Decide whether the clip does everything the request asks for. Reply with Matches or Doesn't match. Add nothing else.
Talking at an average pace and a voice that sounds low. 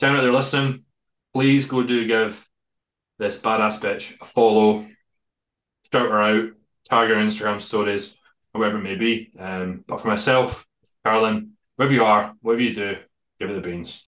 Matches